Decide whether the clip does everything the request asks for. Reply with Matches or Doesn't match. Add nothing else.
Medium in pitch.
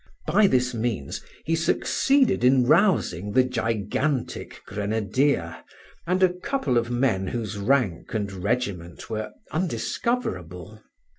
Doesn't match